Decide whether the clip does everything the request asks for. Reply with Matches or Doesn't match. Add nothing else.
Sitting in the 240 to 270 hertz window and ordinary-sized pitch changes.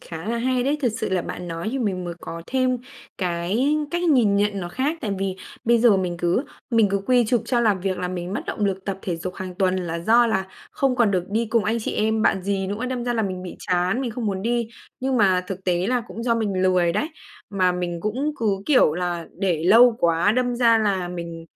Doesn't match